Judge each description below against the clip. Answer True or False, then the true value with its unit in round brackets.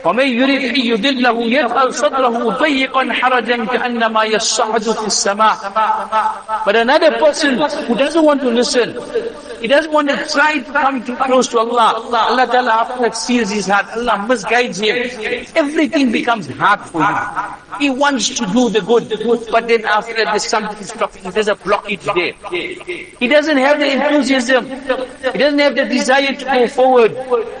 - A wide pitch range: False (3.7 semitones)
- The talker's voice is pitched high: True (250 Hz)